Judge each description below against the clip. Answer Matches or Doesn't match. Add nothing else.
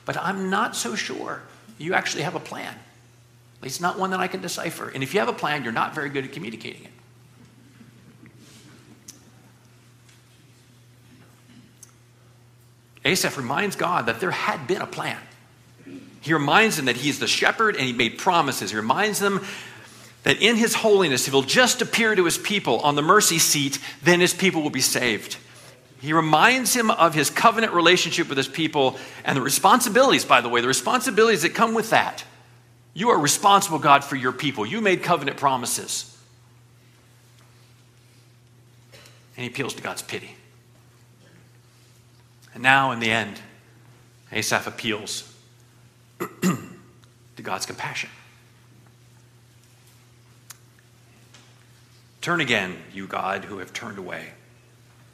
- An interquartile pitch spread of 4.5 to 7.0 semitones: Matches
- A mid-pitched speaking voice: Doesn't match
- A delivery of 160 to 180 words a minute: Doesn't match